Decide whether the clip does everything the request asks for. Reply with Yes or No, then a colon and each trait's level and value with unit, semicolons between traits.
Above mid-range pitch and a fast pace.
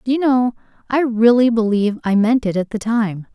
Yes: high, 230 Hz; fast, 215 wpm